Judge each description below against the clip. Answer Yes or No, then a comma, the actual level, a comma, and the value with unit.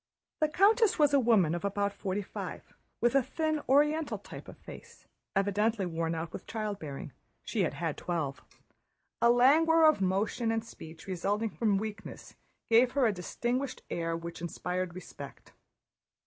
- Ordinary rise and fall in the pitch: No, wide, 6.5 semitones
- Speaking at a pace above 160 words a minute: No, average, 150 wpm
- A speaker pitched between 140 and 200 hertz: No, high, 210 Hz